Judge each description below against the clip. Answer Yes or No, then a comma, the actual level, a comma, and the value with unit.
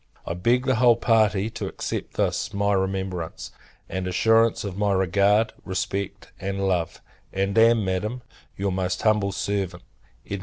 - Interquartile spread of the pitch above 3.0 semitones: No, narrow, 2.5 semitones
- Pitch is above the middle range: No, low, 100 Hz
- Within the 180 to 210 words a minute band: No, average, 150 wpm